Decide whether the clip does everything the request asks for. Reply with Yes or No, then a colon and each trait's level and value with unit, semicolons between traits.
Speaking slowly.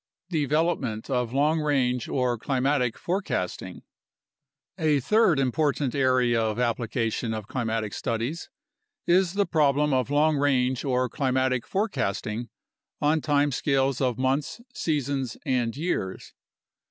Yes: slow, 115 wpm